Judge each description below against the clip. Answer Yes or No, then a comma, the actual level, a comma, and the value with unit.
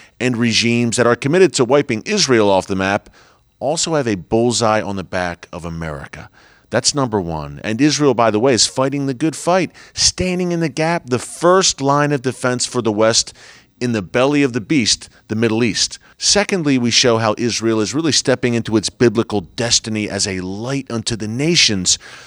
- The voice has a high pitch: No, low, 120 Hz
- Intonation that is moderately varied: Yes, average, 4.5 semitones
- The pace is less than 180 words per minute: No, average, 195 wpm